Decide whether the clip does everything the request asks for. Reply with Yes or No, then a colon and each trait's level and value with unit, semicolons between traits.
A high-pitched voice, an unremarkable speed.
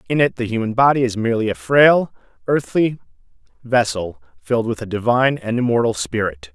No: low, 115 Hz; average, 165 wpm